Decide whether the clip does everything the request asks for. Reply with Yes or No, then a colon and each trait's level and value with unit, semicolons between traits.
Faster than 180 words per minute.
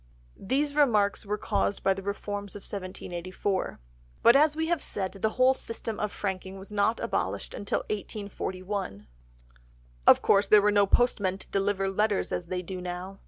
No: average, 165 wpm